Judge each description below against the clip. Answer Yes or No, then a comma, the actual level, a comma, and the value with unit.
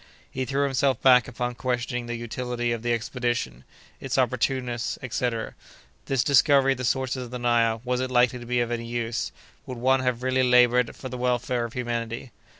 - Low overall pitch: Yes, low, 125 Hz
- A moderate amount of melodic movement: No, narrow, 1.4 semitones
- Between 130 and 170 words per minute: No, average, 180 wpm